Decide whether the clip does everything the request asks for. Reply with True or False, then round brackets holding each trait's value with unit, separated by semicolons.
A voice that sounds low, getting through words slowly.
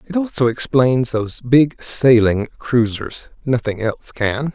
True (125 Hz; 130 wpm)